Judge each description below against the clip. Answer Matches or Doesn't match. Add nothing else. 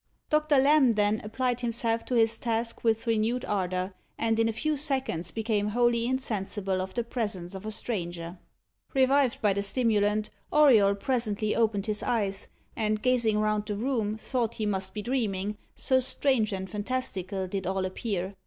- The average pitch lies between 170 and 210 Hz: Doesn't match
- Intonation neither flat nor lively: Matches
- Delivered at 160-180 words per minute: Matches